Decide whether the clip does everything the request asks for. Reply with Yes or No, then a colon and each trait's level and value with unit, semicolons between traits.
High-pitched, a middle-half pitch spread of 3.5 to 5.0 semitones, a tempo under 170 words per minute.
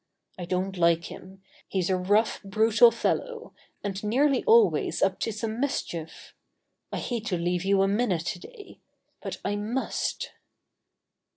Yes: high, 205 Hz; average, 4.3 semitones; average, 145 wpm